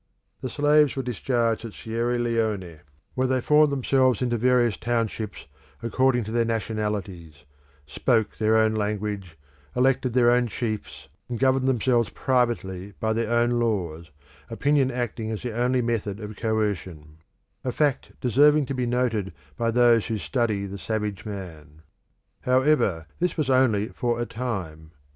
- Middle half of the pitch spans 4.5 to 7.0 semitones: No, average, 3.4 semitones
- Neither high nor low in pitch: No, low, 115 Hz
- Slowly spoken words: No, average, 145 wpm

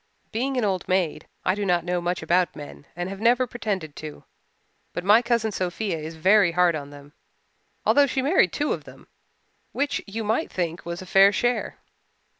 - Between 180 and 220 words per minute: Yes, average, 190 wpm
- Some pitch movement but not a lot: Yes, average, 4.6 semitones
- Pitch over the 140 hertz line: Yes, medium, 185 Hz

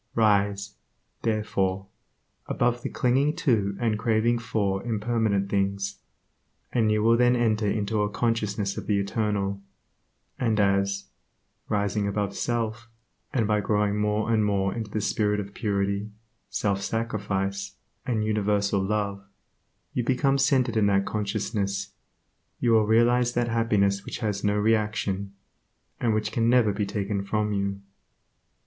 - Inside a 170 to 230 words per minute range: No, average, 140 wpm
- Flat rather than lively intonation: Yes, narrow, 2.3 semitones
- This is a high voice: No, low, 105 Hz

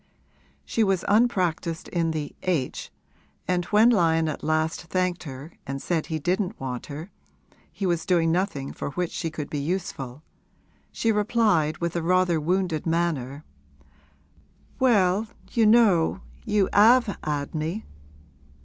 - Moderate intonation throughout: Yes, average, 3.8 semitones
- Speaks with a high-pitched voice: No, medium, 170 Hz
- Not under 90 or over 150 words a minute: Yes, average, 140 wpm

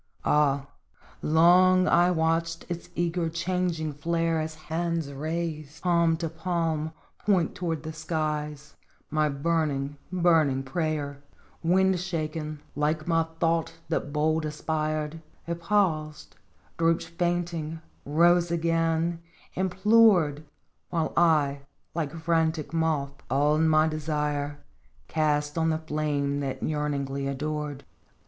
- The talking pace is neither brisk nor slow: No, slow, 110 wpm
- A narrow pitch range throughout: Yes, narrow, 2.1 semitones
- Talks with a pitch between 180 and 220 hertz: No, medium, 160 Hz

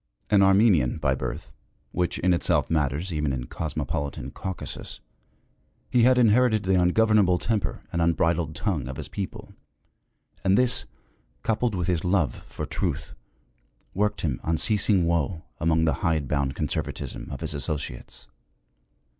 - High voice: No, very low, 85 Hz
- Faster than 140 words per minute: No, slow, 135 wpm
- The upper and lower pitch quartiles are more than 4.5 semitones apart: Yes, average, 4.9 semitones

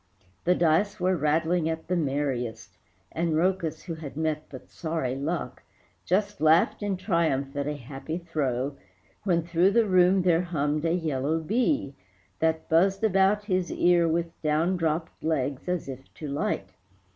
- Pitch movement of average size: Yes, average, 3.3 semitones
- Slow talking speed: No, average, 155 wpm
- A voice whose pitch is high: No, medium, 165 Hz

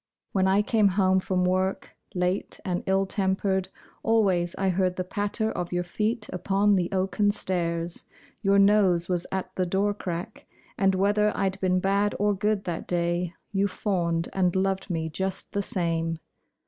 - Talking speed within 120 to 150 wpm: No, average, 165 wpm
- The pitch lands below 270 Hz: Yes, high, 190 Hz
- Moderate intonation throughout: No, narrow, 2.0 semitones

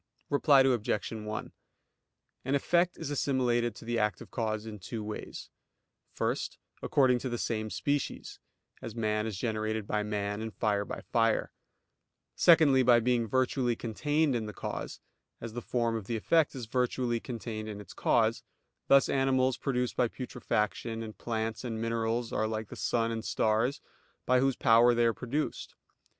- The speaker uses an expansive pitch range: No, average, 2.8 semitones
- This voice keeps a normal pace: Yes, average, 165 wpm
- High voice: No, low, 115 Hz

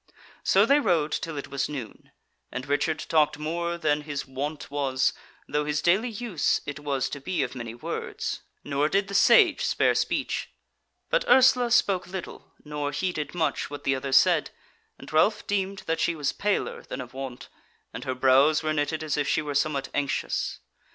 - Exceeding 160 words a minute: Yes, average, 185 wpm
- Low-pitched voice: No, medium, 150 Hz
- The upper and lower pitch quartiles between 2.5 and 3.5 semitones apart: No, average, 4.1 semitones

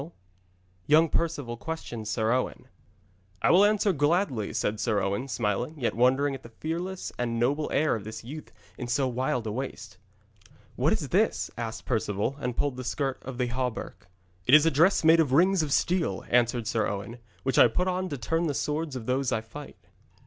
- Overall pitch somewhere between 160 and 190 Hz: No, low, 130 Hz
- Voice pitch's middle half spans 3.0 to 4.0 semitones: No, average, 5.2 semitones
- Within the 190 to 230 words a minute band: Yes, average, 195 wpm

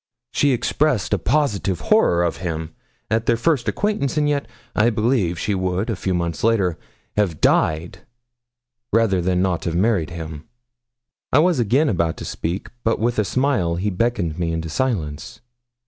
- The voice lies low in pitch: Yes, very low, 95 Hz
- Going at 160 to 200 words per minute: Yes, average, 165 wpm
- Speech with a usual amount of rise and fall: No, wide, 5.9 semitones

